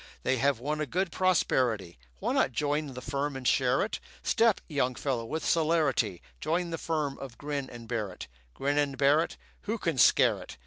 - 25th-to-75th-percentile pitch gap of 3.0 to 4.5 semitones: Yes, average, 4.0 semitones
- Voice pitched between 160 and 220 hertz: No, medium, 145 Hz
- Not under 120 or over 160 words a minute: No, average, 185 wpm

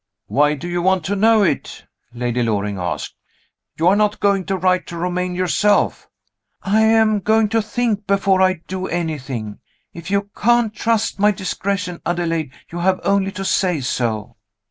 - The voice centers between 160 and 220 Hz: Yes, medium, 185 Hz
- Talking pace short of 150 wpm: No, average, 165 wpm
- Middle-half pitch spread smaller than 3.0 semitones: No, average, 3.8 semitones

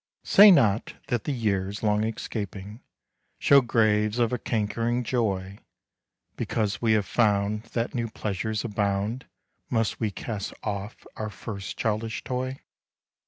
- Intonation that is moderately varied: No, narrow, 2.3 semitones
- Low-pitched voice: Yes, low, 110 Hz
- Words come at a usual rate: No, slow, 130 wpm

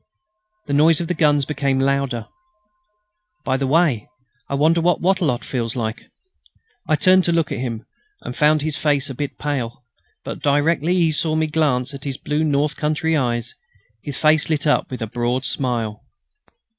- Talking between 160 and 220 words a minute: Yes, average, 175 wpm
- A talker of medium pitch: Yes, medium, 145 Hz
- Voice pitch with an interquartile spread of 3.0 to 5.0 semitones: Yes, average, 3.5 semitones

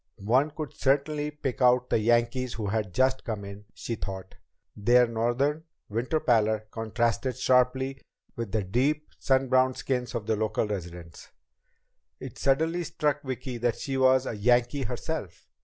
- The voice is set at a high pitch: No, low, 125 Hz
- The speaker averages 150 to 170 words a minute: Yes, average, 155 wpm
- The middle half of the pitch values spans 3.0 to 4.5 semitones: Yes, average, 3.4 semitones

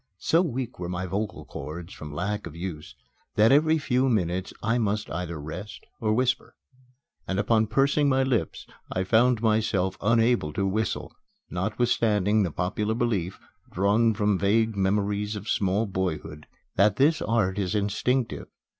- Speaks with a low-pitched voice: Yes, low, 105 Hz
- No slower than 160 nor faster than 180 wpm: No, average, 150 wpm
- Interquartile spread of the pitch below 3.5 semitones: No, average, 3.8 semitones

